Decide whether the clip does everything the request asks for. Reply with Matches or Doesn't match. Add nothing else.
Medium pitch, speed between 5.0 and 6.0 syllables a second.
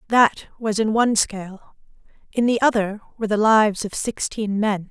Doesn't match